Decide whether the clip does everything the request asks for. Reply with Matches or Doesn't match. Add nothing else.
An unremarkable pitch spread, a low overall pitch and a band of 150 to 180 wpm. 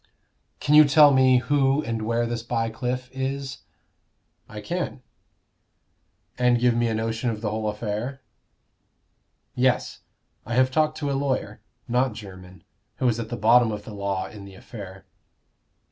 Matches